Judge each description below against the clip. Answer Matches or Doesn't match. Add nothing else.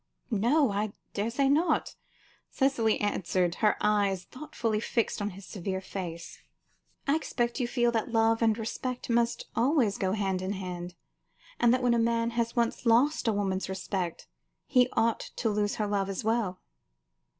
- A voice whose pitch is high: Matches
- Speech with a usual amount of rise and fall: Matches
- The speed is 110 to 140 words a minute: Doesn't match